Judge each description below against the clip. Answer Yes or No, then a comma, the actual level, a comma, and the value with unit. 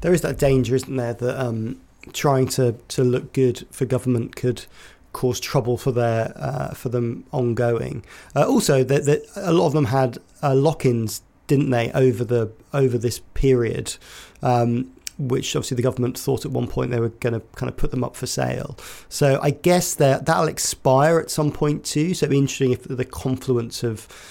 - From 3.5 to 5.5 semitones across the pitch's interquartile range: No, average, 2.7 semitones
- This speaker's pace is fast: No, average, 195 wpm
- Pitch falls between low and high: No, low, 130 Hz